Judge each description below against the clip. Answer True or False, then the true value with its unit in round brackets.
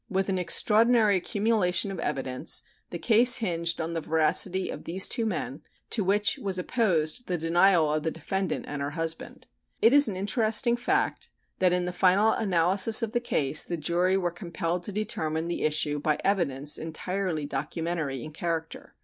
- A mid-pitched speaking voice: True (180 Hz)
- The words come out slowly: False (175 wpm)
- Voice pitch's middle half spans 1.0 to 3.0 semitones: False (4.1 semitones)